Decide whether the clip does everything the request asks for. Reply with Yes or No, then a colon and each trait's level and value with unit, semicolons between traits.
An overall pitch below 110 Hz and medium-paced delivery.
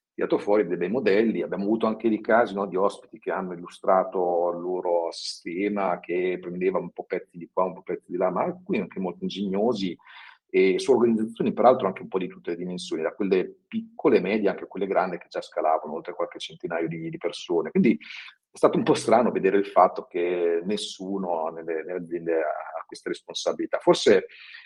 No: low, 100 Hz; fast, 200 wpm